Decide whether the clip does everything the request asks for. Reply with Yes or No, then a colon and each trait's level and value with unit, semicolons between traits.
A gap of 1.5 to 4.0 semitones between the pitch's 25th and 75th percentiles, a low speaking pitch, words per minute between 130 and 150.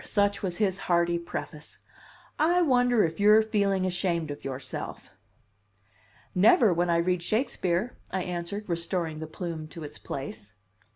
No: average, 3.5 semitones; medium, 180 Hz; average, 140 wpm